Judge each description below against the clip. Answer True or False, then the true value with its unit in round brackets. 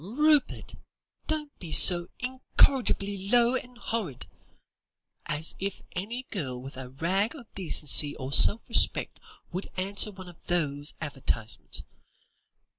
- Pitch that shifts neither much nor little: False (7.9 semitones)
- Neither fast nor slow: False (120 wpm)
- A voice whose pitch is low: False (190 Hz)